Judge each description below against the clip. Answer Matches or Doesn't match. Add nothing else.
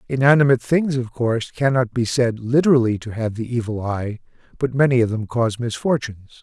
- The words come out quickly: Doesn't match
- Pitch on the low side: Matches